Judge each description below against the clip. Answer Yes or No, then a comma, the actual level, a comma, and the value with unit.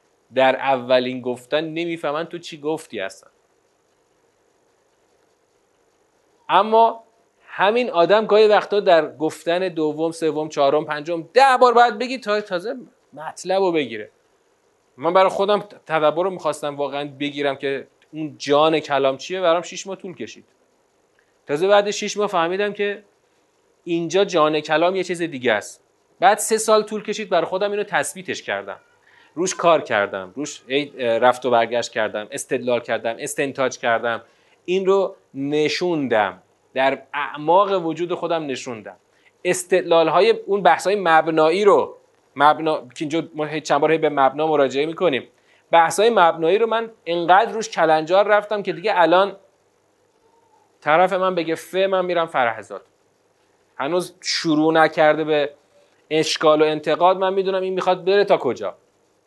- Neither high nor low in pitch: Yes, medium, 175 Hz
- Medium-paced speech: Yes, average, 140 wpm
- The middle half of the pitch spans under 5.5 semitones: No, wide, 5.9 semitones